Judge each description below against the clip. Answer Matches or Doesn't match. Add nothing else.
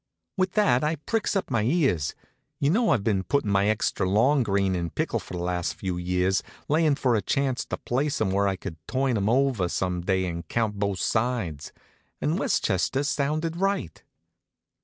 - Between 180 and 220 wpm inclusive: Matches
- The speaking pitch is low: Matches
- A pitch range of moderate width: Doesn't match